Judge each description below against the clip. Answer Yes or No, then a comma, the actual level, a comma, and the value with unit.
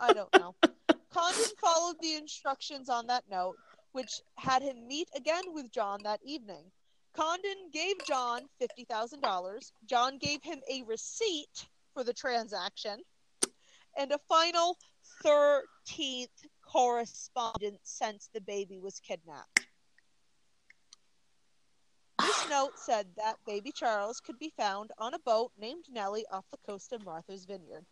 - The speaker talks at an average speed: No, slow, 130 wpm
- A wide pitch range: Yes, wide, 6.5 semitones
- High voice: Yes, very high, 265 Hz